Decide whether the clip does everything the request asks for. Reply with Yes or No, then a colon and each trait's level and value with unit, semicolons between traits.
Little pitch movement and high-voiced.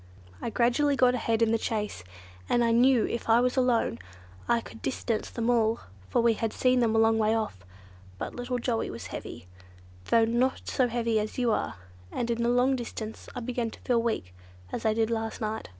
Yes: narrow, 1.6 semitones; high, 230 Hz